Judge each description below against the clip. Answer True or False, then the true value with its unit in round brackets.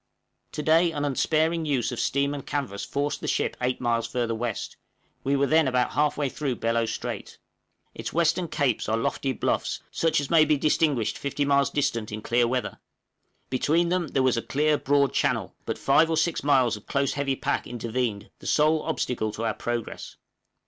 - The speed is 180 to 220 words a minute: True (190 wpm)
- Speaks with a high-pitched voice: False (140 Hz)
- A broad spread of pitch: False (4.0 semitones)